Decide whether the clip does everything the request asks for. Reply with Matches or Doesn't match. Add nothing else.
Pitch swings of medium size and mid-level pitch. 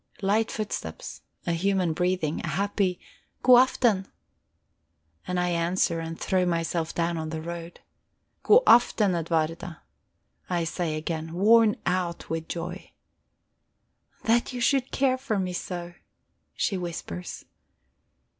Matches